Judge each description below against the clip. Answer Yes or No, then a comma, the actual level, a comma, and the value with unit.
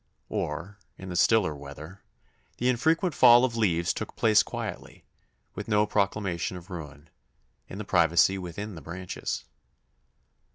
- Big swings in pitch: No, average, 4.1 semitones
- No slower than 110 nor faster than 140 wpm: Yes, slow, 135 wpm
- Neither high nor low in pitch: No, very low, 95 Hz